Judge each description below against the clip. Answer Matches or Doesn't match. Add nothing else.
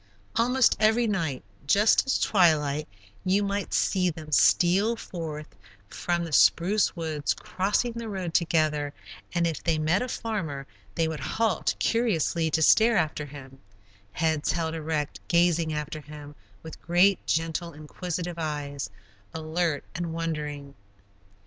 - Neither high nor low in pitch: Matches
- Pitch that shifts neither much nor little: Matches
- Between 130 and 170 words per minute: Matches